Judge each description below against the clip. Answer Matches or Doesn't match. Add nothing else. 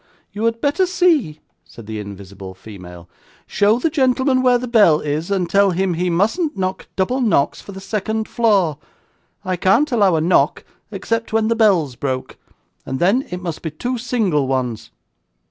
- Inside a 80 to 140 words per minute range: Doesn't match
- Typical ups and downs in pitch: Doesn't match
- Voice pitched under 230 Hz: Matches